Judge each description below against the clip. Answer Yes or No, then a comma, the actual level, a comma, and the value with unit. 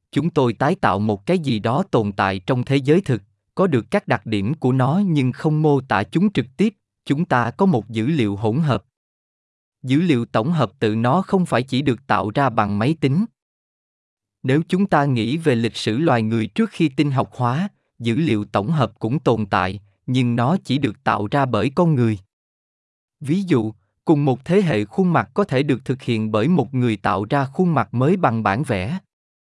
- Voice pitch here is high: No, low, 130 Hz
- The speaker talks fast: No, average, 215 wpm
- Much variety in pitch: Yes, wide, 6.2 semitones